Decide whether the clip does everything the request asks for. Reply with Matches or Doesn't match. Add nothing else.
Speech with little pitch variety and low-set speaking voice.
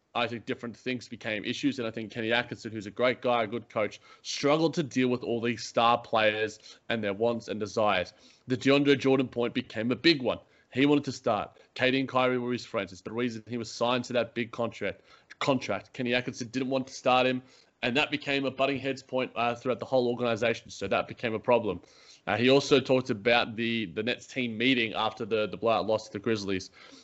Matches